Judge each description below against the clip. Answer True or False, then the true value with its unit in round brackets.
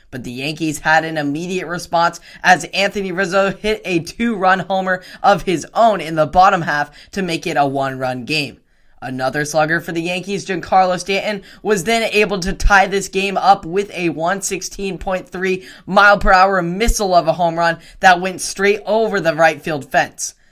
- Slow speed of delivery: False (180 wpm)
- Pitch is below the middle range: False (185 Hz)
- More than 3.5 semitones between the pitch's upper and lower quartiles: False (3.2 semitones)